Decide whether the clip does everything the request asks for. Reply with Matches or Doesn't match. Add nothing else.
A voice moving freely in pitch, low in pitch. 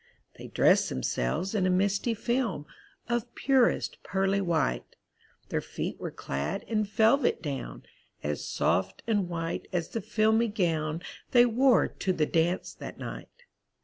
Doesn't match